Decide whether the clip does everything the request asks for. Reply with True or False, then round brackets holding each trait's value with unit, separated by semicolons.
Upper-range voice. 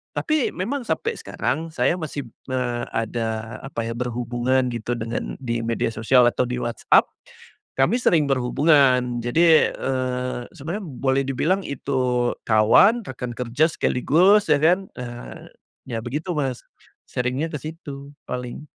False (130 Hz)